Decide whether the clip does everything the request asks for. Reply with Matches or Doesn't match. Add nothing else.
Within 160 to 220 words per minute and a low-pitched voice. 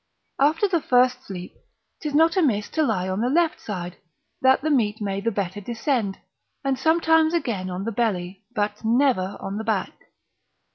Doesn't match